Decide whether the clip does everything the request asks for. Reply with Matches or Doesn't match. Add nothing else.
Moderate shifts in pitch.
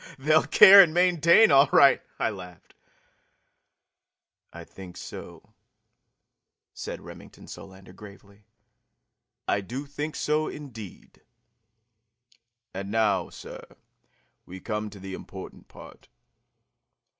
Doesn't match